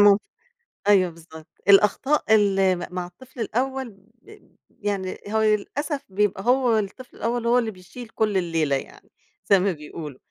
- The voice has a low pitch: No, high, 205 Hz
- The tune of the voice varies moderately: Yes, average, 4.3 semitones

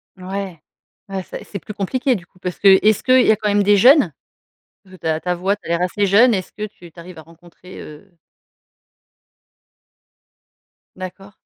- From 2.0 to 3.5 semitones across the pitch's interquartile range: Yes, average, 2.8 semitones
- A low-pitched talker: No, high, 190 Hz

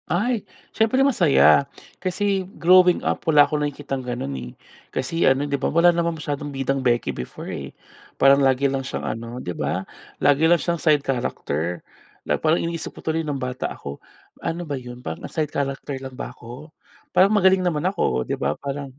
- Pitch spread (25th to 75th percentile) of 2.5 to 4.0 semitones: No, average, 4.7 semitones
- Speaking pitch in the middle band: Yes, medium, 145 Hz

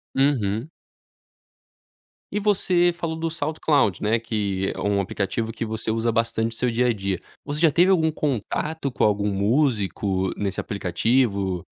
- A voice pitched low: Yes, low, 115 Hz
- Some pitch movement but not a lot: No, wide, 6.7 semitones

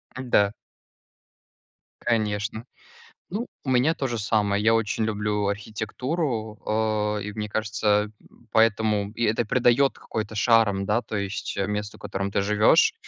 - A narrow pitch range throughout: Yes, narrow, 1.7 semitones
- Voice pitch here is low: Yes, low, 110 Hz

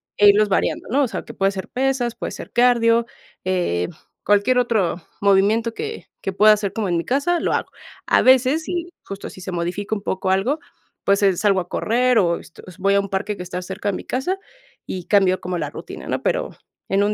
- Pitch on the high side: Yes, high, 205 Hz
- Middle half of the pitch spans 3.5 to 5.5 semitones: Yes, average, 4.1 semitones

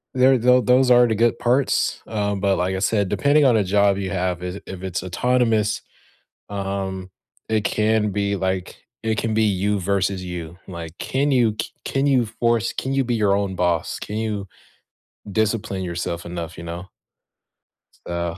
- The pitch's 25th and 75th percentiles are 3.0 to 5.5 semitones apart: Yes, average, 3.7 semitones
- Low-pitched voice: Yes, low, 100 Hz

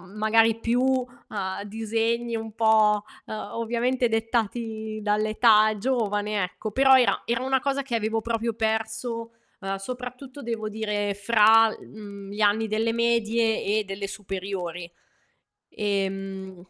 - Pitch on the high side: Yes, high, 220 Hz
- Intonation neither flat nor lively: No, narrow, 2.1 semitones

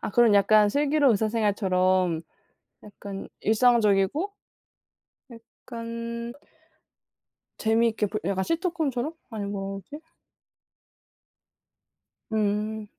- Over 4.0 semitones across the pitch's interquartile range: No, average, 2.9 semitones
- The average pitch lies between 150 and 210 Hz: No, high, 220 Hz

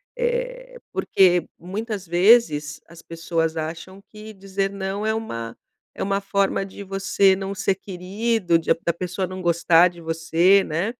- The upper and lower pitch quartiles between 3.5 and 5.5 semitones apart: No, average, 2.9 semitones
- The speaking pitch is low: No, high, 190 Hz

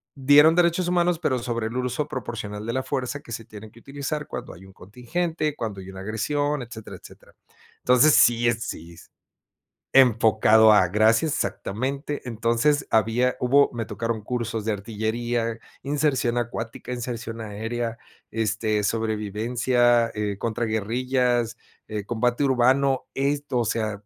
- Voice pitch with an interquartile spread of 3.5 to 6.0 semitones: No, average, 3.1 semitones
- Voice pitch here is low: Yes, low, 120 Hz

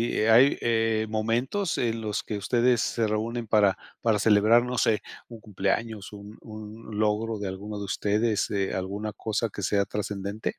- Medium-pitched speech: No, low, 110 Hz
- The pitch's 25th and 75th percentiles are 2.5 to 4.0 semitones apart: No, narrow, 1.8 semitones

